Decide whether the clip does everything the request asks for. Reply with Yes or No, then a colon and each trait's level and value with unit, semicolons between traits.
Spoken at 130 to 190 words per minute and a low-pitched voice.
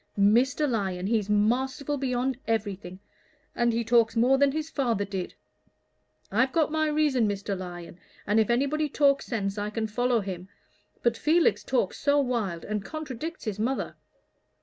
No: average, 155 wpm; high, 235 Hz